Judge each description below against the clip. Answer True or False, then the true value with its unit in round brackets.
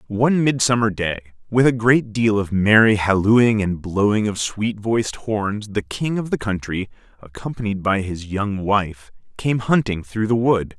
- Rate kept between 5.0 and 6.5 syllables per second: False (4.4 syllables/s)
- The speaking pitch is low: True (105 Hz)